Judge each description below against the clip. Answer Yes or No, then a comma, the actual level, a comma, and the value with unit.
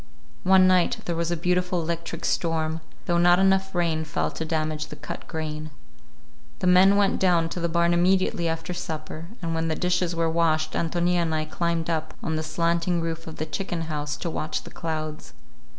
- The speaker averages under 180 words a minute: No, average, 195 wpm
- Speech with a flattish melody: Yes, narrow, 1.9 semitones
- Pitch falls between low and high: Yes, medium, 165 Hz